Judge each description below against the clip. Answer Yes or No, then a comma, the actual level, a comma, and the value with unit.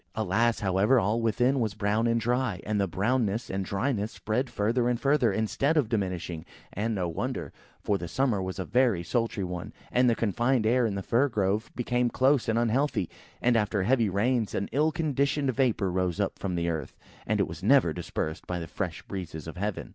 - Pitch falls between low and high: No, low, 110 Hz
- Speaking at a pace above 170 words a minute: Yes, average, 200 wpm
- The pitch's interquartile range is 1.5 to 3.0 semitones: No, average, 4.4 semitones